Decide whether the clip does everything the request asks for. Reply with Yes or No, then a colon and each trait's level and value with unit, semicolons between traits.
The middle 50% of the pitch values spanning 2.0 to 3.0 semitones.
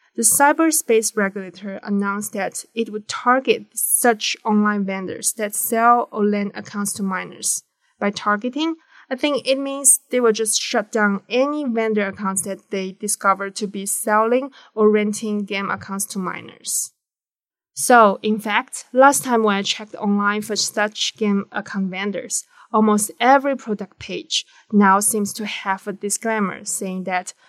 Yes: average, 2.7 semitones